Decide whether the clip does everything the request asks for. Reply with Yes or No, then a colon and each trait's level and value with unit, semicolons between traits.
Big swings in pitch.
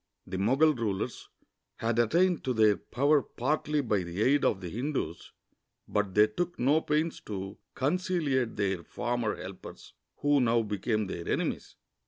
Yes: wide, 5.9 semitones